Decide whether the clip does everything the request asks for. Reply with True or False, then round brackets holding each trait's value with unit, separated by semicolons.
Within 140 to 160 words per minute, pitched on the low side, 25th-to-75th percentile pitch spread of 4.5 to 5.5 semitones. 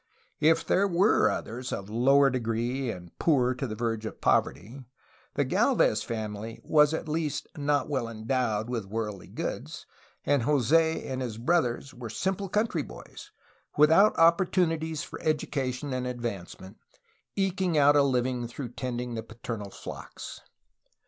True (145 wpm; 130 Hz; 5.1 semitones)